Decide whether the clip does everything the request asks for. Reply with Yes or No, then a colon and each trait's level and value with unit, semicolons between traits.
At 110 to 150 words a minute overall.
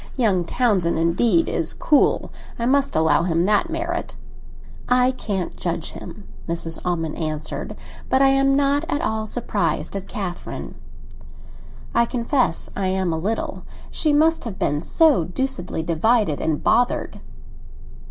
Yes: average, 140 wpm